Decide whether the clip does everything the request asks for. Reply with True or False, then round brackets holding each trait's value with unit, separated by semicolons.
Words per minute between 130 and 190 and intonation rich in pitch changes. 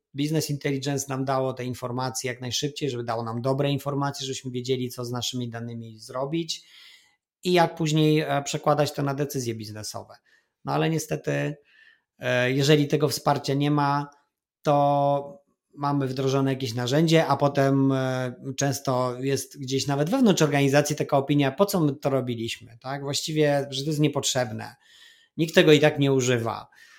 False (150 wpm; 2.5 semitones)